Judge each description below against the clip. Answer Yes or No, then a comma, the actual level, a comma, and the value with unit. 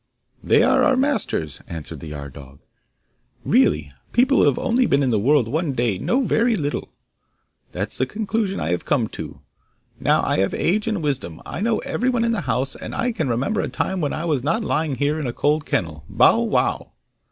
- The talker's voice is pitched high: No, medium, 145 Hz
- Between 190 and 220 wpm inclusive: Yes, fast, 205 wpm